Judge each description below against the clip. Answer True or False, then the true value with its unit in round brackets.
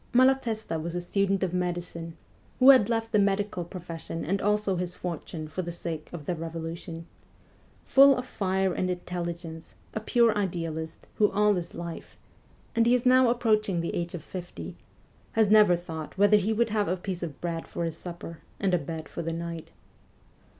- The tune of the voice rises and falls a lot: False (3.9 semitones)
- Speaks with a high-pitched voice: False (180 Hz)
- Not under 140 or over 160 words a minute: False (185 wpm)